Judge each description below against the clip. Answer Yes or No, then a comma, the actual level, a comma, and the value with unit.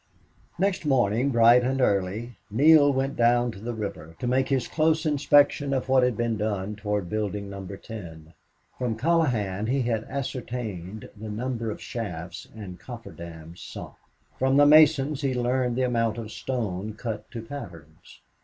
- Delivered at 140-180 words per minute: Yes, average, 160 wpm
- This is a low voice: Yes, low, 115 Hz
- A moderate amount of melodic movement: Yes, average, 4.4 semitones